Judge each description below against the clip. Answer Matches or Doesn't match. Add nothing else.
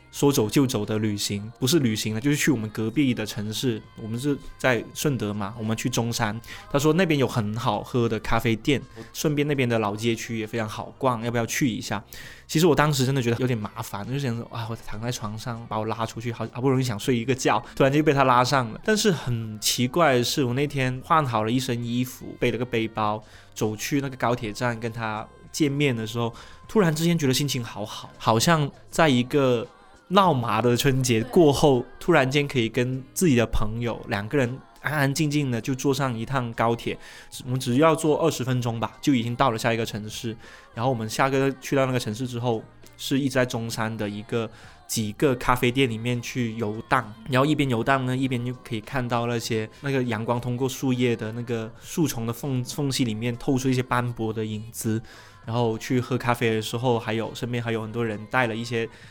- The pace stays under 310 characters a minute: Doesn't match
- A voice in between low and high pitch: Doesn't match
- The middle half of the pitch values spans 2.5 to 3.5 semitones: Matches